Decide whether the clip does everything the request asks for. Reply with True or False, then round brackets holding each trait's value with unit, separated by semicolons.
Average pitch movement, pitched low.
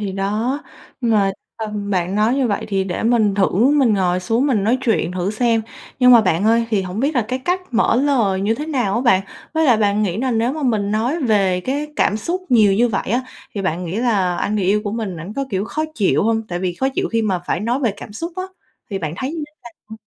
False (4.2 semitones; 220 Hz)